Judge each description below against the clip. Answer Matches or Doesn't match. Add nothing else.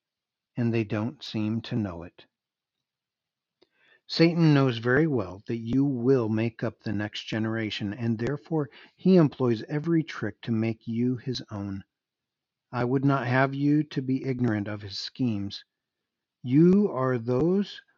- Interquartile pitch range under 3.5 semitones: Doesn't match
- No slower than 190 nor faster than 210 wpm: Doesn't match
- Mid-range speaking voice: Doesn't match